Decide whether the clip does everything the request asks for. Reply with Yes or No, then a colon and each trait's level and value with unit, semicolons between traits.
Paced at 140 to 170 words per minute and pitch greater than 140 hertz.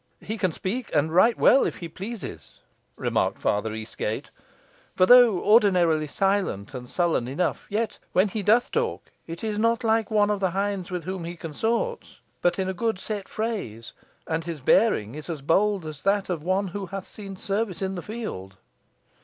No: average, 180 wpm; high, 190 Hz